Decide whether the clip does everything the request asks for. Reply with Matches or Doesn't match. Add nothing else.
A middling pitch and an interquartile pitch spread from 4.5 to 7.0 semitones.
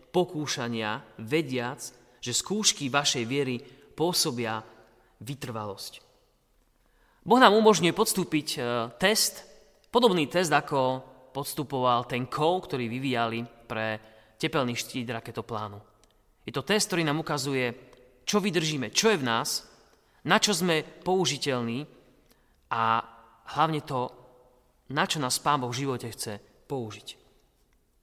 Doesn't match